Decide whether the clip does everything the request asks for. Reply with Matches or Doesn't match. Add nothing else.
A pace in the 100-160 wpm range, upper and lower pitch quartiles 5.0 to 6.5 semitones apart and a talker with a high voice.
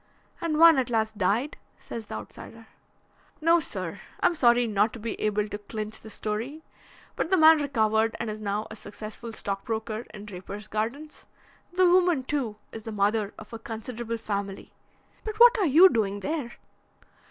Doesn't match